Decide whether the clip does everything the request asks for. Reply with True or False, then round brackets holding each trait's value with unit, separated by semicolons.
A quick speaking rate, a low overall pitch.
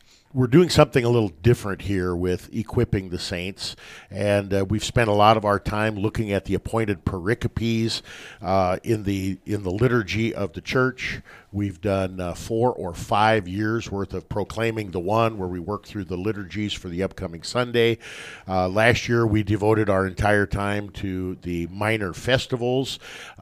False (175 wpm; 105 Hz)